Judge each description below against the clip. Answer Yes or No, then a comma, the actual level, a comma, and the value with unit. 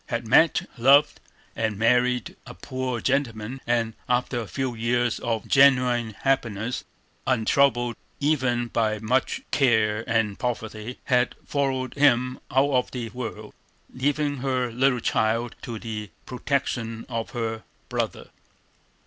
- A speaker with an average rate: No, slow, 125 wpm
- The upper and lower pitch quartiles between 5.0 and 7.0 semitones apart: No, narrow, 2.6 semitones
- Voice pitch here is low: Yes, low, 120 Hz